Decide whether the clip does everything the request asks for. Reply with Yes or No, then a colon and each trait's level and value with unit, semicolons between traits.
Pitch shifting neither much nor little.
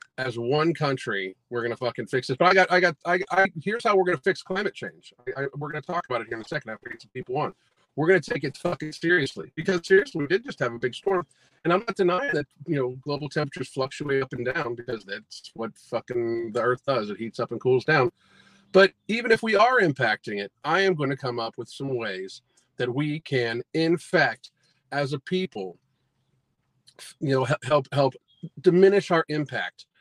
No: wide, 5.9 semitones